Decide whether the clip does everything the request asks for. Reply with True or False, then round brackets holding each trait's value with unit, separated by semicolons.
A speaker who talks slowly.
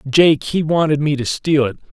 False (210 wpm)